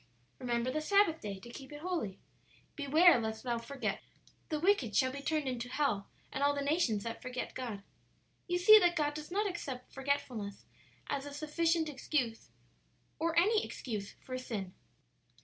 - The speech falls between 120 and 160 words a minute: No, average, 175 wpm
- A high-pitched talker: Yes, very high, 280 Hz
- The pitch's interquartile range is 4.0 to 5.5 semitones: Yes, average, 5.2 semitones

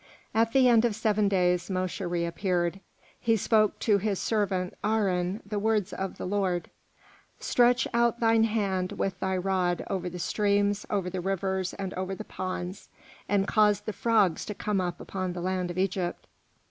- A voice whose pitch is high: Yes, high, 195 Hz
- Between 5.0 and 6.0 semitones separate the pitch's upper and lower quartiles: No, narrow, 2.6 semitones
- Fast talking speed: No, average, 170 wpm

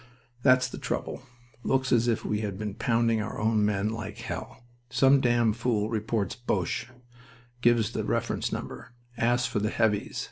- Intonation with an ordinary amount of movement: No, narrow, 2.3 semitones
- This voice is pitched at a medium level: No, low, 115 Hz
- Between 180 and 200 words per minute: No, average, 165 wpm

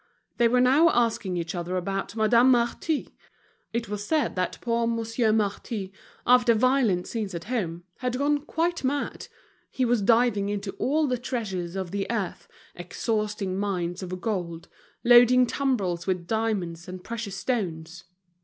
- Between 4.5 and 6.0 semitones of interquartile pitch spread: Yes, average, 4.8 semitones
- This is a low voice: No, high, 220 Hz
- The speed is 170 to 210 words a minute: No, average, 150 wpm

